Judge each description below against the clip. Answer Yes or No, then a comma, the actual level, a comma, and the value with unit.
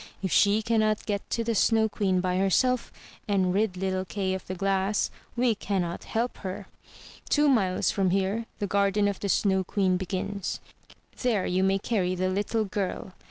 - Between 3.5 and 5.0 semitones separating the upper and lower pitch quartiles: No, narrow, 2.4 semitones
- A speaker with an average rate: Yes, average, 175 wpm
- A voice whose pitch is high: Yes, high, 195 Hz